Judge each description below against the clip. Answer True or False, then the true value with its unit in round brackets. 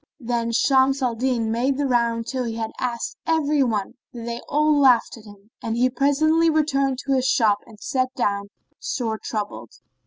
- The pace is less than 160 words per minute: False (185 wpm)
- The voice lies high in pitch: True (245 Hz)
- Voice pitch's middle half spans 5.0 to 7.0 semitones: False (3.2 semitones)